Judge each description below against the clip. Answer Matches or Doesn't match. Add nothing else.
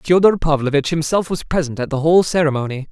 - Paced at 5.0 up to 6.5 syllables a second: Matches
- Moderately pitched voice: Matches